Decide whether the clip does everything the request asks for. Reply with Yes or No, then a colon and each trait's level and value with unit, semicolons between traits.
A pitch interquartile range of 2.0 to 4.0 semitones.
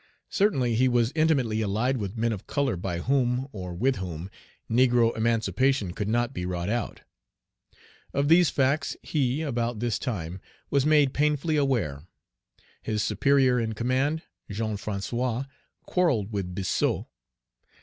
No: average, 4.8 semitones